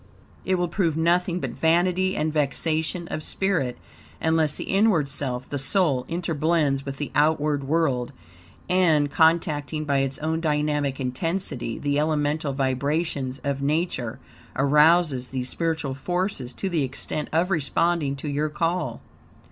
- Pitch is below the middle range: No, medium, 150 Hz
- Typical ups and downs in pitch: Yes, average, 3.3 semitones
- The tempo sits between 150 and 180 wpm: No, average, 140 wpm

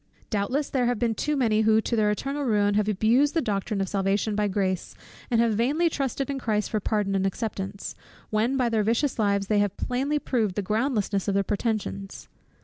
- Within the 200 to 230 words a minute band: Yes, fast, 205 wpm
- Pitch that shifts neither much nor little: Yes, average, 3.5 semitones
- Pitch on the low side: No, high, 215 Hz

